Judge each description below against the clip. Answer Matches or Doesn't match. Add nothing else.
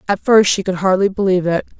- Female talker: Matches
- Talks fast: Matches